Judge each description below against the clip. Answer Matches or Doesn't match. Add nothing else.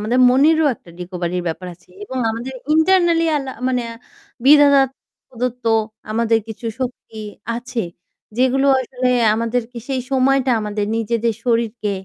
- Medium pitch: Doesn't match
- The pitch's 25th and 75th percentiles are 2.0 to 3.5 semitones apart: Matches